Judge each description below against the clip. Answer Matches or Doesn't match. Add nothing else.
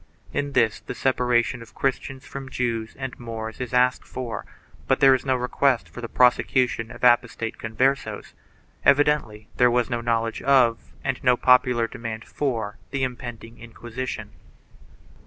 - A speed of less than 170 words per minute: Matches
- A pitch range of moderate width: Doesn't match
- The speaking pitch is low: Matches